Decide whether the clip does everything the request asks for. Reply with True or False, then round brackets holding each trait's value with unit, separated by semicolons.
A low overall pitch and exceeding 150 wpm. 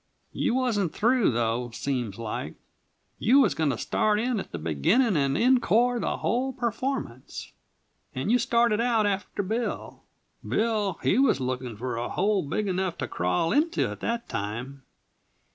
False (200 Hz; 160 wpm)